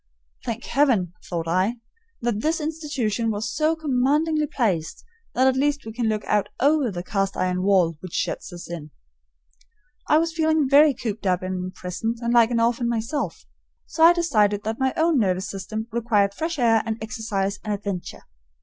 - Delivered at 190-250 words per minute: No, average, 175 wpm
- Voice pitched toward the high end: Yes, high, 225 Hz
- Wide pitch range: Yes, wide, 6.2 semitones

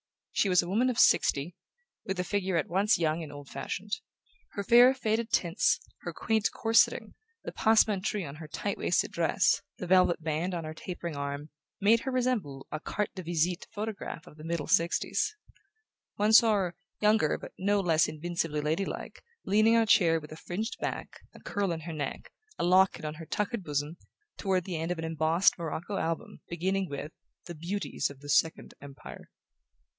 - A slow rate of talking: No, average, 185 wpm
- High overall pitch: No, medium, 175 Hz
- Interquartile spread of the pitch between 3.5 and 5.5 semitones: Yes, average, 4.4 semitones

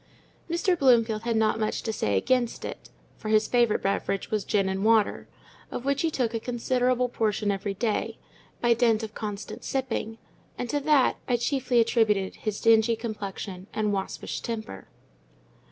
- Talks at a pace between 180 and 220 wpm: No, average, 160 wpm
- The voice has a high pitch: Yes, high, 225 Hz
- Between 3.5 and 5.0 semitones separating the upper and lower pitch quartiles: No, average, 2.7 semitones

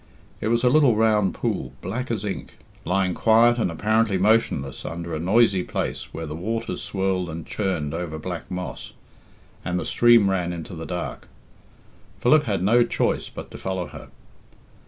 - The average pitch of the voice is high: No, very low, 95 Hz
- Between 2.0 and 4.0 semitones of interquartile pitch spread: No, average, 4.5 semitones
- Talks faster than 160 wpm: Yes, average, 170 wpm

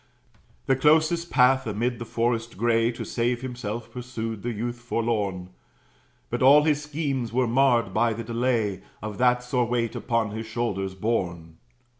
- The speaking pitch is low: Yes, low, 120 Hz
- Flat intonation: Yes, narrow, 2.2 semitones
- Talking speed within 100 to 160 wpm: Yes, average, 155 wpm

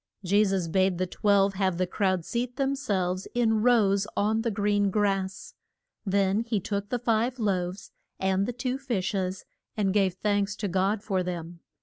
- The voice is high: Yes, high, 200 Hz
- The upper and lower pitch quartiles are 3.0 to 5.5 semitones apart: No, narrow, 2.5 semitones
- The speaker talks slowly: No, average, 180 wpm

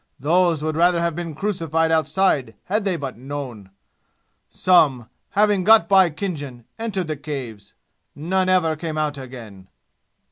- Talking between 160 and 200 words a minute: No, average, 140 wpm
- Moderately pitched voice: Yes, medium, 160 Hz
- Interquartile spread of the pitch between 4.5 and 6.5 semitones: Yes, average, 5.1 semitones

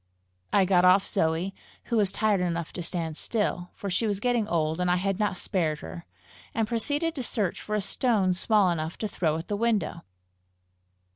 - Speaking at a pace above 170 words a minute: Yes, average, 195 wpm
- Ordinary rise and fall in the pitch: Yes, average, 3.8 semitones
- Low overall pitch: No, high, 190 Hz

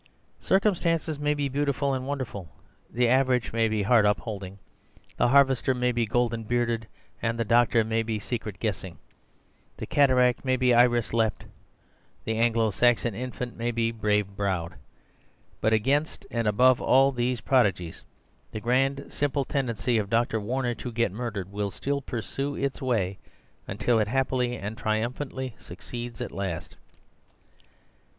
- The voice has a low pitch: Yes, low, 120 Hz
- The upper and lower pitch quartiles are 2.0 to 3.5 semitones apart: Yes, average, 3.0 semitones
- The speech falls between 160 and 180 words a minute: No, average, 145 wpm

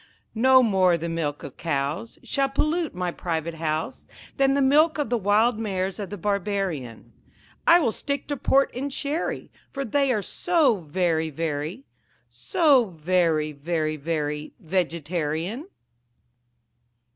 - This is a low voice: No, medium, 185 Hz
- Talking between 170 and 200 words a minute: No, slow, 135 wpm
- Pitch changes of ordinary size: No, wide, 8.8 semitones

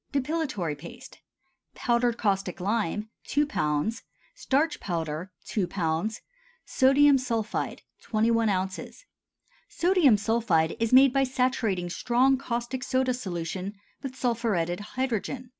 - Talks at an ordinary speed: No, slow, 110 wpm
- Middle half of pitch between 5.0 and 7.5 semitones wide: Yes, wide, 5.6 semitones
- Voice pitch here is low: No, high, 230 Hz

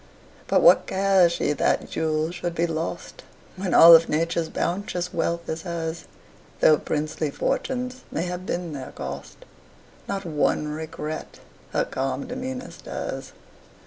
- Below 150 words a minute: Yes, average, 140 wpm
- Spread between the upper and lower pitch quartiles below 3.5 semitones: Yes, narrow, 2.5 semitones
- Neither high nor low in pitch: Yes, medium, 170 Hz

